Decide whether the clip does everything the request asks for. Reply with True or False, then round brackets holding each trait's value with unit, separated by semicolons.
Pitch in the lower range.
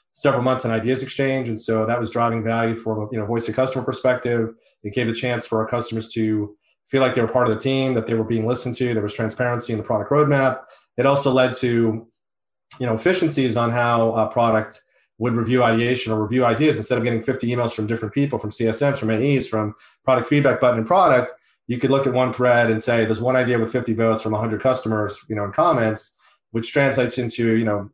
True (120 Hz)